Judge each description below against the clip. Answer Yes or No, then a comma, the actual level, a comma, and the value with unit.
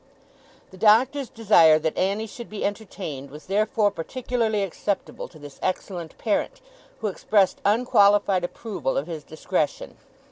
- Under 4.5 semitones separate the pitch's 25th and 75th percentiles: No, average, 4.8 semitones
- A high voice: Yes, high, 200 Hz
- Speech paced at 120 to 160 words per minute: Yes, slow, 135 wpm